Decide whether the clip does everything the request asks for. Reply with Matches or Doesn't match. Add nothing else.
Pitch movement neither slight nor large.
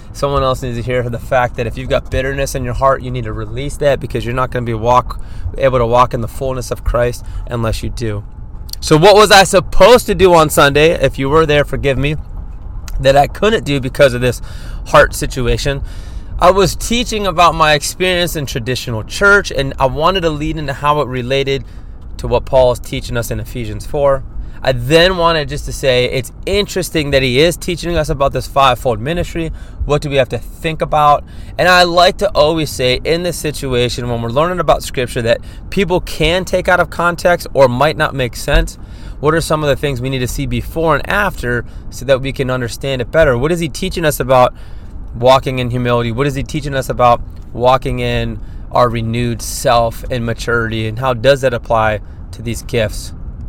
Matches